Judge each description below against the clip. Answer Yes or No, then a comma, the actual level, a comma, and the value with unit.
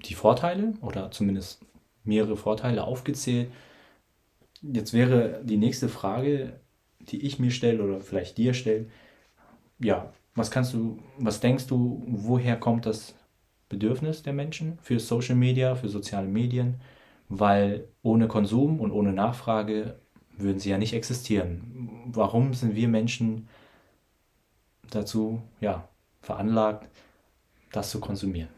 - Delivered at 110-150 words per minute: Yes, slow, 125 wpm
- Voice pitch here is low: Yes, low, 115 Hz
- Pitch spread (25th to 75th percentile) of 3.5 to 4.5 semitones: No, average, 2.8 semitones